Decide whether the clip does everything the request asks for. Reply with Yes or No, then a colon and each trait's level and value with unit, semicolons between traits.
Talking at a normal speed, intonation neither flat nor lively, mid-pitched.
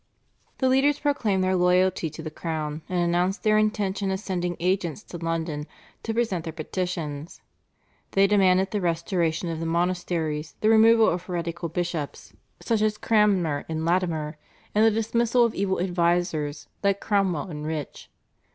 Yes: average, 155 wpm; average, 3.7 semitones; medium, 180 Hz